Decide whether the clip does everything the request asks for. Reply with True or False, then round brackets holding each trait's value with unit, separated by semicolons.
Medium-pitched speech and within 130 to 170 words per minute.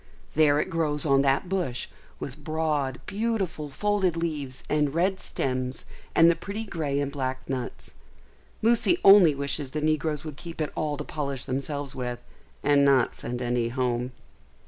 True (145 Hz; 160 wpm)